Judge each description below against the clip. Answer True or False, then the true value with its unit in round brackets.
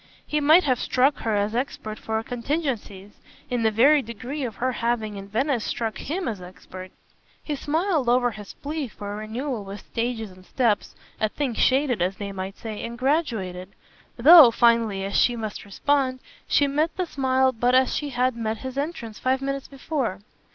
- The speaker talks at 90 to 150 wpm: False (185 wpm)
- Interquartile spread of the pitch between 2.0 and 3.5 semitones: False (4.4 semitones)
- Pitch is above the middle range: True (240 Hz)